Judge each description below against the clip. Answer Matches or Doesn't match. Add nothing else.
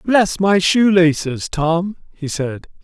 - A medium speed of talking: Matches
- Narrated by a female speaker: Doesn't match